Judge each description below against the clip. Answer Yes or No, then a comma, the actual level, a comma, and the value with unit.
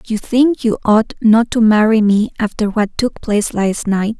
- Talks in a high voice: Yes, high, 220 Hz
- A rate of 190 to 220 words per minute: Yes, average, 200 wpm